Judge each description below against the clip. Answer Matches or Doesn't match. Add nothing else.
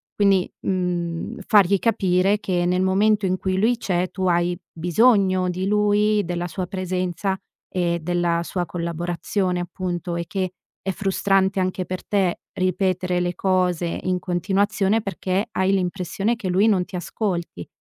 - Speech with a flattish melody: Matches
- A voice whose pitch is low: Doesn't match